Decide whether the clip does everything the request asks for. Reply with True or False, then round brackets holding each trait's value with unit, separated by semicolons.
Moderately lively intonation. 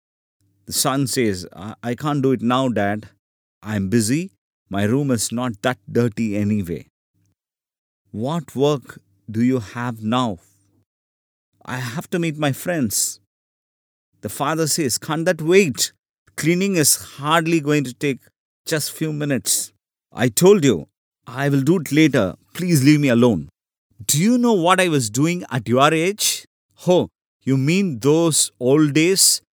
False (6.6 semitones)